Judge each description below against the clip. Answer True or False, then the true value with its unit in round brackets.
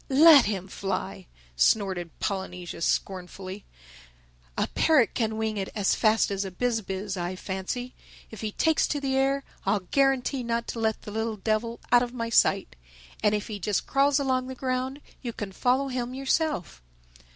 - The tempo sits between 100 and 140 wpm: False (175 wpm)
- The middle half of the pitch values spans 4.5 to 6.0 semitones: True (5.0 semitones)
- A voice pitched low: False (220 Hz)